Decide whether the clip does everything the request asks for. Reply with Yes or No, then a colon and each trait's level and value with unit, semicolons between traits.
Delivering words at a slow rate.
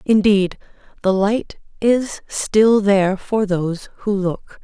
Yes: slow, 130 wpm